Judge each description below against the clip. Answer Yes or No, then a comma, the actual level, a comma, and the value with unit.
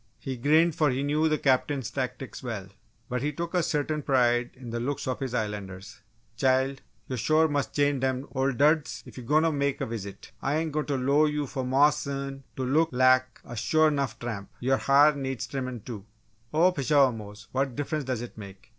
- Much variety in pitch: No, average, 3.0 semitones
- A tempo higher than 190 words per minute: Yes, fast, 205 wpm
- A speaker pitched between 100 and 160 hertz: Yes, low, 135 Hz